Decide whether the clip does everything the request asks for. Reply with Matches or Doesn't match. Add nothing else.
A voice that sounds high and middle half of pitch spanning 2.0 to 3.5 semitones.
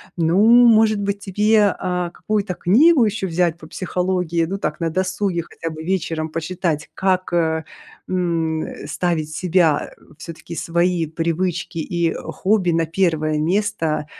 Doesn't match